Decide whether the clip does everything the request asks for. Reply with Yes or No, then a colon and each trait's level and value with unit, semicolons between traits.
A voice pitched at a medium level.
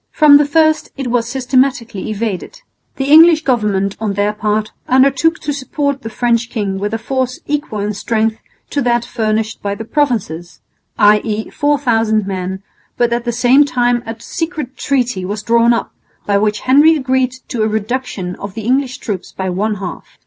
No: high, 235 Hz